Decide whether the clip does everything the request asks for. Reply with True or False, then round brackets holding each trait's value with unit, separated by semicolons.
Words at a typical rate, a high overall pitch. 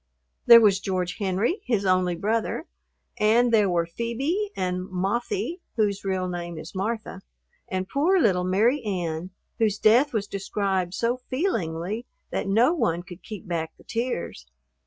True (150 wpm; 200 Hz)